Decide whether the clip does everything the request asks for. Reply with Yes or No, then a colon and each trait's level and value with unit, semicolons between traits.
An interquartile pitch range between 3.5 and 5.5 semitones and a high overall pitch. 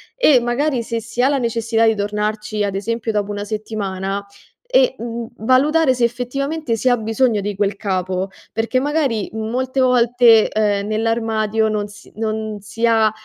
No: average, 2.8 semitones; high, 225 Hz